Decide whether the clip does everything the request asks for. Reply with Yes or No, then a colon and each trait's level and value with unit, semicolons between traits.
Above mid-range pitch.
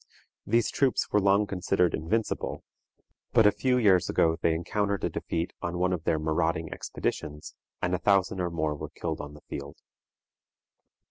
No: very low, 90 Hz